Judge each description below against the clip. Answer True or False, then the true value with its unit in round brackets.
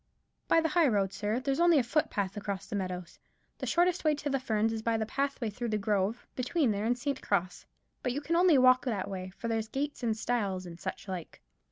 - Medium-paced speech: False (225 wpm)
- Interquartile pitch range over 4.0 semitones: True (5.4 semitones)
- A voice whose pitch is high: True (230 Hz)